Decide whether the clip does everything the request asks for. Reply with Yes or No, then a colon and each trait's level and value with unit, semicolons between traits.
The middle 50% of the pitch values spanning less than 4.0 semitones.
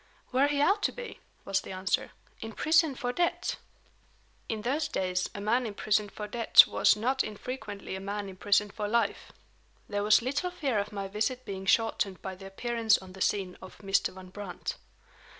No: average, 4.3 semitones